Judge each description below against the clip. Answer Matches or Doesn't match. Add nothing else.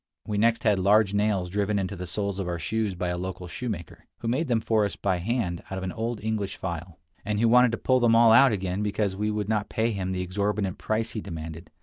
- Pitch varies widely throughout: Doesn't match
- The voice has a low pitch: Matches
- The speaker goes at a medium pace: Doesn't match